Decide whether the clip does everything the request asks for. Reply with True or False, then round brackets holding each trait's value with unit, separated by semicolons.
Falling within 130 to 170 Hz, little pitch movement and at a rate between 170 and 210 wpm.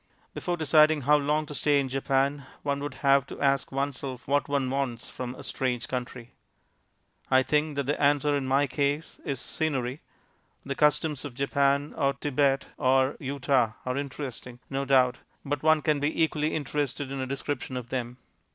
True (140 Hz; 1.9 semitones; 175 wpm)